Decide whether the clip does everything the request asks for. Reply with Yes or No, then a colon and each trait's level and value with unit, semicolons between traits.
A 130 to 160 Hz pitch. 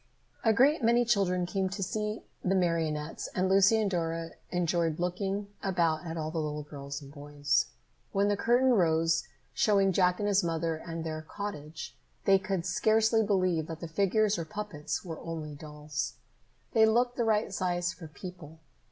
No: medium, 180 Hz